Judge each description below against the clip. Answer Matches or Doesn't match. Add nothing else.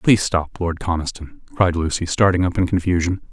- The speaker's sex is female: Doesn't match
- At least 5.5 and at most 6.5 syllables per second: Matches